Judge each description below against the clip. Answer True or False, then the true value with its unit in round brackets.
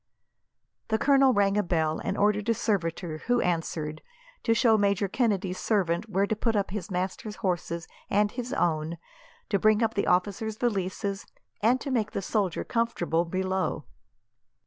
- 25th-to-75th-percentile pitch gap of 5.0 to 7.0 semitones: False (3.6 semitones)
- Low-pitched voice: False (200 Hz)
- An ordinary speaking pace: True (160 wpm)